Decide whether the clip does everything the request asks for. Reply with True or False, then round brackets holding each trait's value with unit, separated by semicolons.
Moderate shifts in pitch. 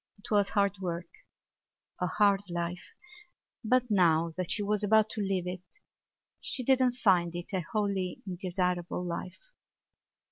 True (3.1 semitones)